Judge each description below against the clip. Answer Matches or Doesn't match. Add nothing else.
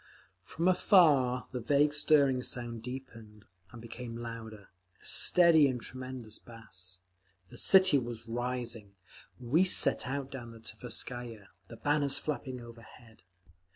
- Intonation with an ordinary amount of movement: Matches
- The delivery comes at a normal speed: Doesn't match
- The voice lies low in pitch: Matches